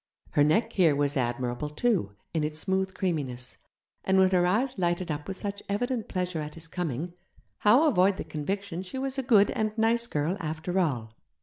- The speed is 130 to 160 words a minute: No, average, 190 wpm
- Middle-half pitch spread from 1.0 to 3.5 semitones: No, average, 5.2 semitones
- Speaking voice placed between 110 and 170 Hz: No, medium, 180 Hz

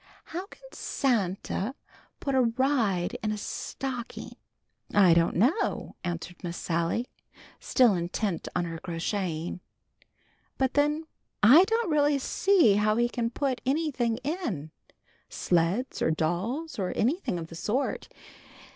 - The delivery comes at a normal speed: No, slow, 130 wpm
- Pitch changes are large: Yes, wide, 7.7 semitones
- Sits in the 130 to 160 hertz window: No, high, 230 Hz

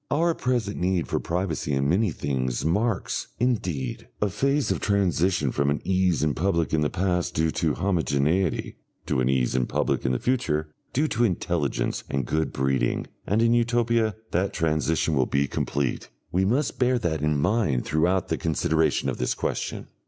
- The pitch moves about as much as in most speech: No, wide, 5.8 semitones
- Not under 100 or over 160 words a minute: No, average, 175 wpm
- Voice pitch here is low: Yes, very low, 85 Hz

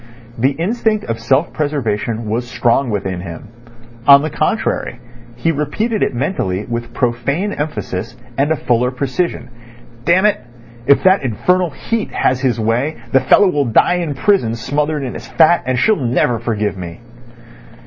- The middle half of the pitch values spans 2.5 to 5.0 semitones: No, wide, 5.4 semitones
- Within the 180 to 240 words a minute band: No, average, 155 wpm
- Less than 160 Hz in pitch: Yes, low, 135 Hz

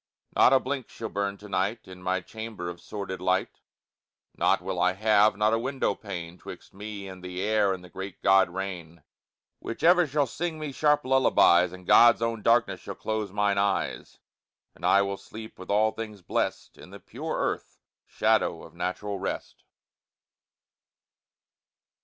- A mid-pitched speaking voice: No, low, 100 Hz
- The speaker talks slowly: No, average, 170 wpm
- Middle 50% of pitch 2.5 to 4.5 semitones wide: Yes, average, 3.4 semitones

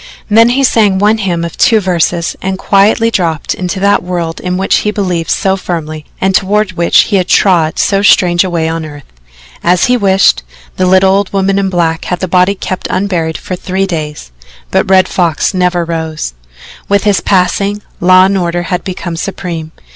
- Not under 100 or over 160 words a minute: No, average, 195 wpm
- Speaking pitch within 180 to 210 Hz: Yes, medium, 185 Hz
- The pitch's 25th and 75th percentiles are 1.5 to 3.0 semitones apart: Yes, narrow, 2.5 semitones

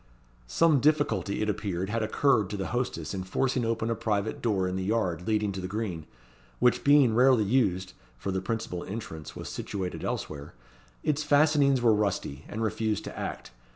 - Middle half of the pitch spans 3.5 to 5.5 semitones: Yes, average, 4.5 semitones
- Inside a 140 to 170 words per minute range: No, average, 180 wpm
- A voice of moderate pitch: No, low, 110 Hz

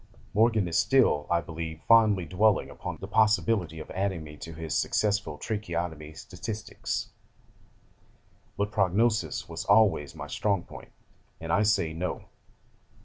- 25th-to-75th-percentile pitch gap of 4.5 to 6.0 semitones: Yes, average, 4.8 semitones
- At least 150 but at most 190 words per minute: No, slow, 135 wpm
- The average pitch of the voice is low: Yes, very low, 95 Hz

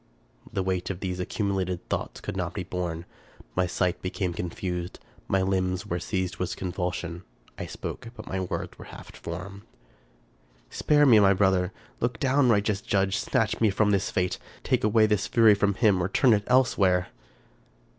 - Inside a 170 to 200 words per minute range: Yes, average, 175 wpm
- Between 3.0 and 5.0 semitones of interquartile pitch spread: No, narrow, 2.4 semitones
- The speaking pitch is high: No, very low, 95 Hz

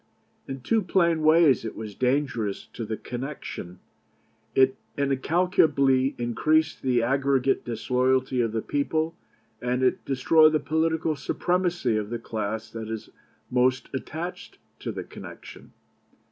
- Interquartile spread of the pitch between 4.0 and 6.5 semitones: Yes, average, 4.7 semitones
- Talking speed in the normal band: No, slow, 130 wpm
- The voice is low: Yes, low, 130 Hz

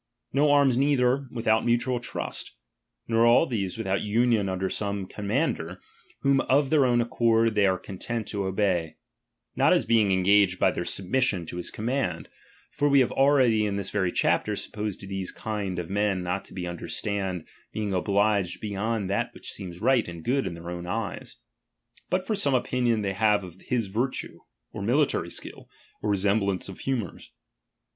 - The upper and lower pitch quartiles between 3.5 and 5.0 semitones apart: Yes, average, 4.3 semitones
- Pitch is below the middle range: Yes, low, 105 Hz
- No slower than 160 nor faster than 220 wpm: Yes, average, 175 wpm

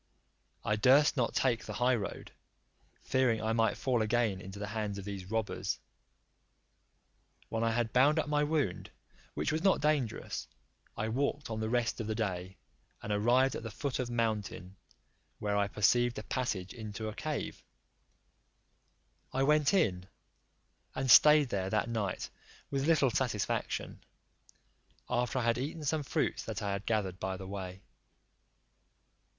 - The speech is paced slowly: No, average, 155 wpm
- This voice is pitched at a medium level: No, low, 115 Hz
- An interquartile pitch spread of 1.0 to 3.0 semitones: No, average, 4.4 semitones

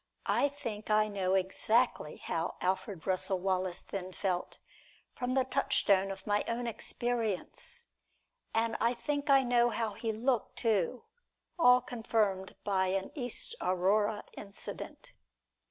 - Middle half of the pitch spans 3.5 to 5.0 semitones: Yes, average, 4.3 semitones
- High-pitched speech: Yes, high, 215 Hz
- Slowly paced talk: Yes, slow, 130 wpm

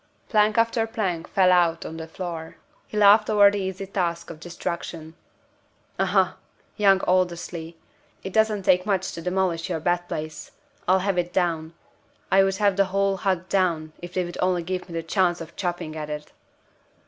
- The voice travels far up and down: No, narrow, 2.5 semitones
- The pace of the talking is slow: No, average, 180 wpm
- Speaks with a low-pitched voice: No, medium, 180 Hz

